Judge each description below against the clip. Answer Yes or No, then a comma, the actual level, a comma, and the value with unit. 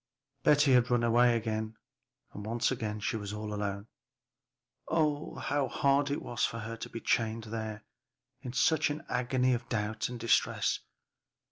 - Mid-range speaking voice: No, low, 115 Hz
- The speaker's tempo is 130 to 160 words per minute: Yes, average, 150 wpm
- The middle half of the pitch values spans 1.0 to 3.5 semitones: Yes, average, 3.0 semitones